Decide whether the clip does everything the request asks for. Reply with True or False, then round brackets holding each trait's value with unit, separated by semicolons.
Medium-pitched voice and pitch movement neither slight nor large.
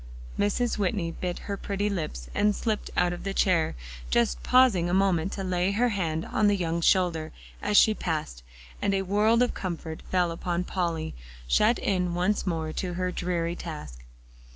True (180 Hz; 3.2 semitones)